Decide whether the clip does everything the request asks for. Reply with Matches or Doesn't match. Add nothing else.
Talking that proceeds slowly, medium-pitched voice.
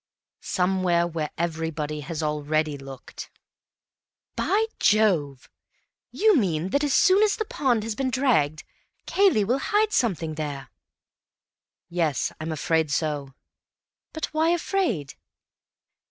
Matches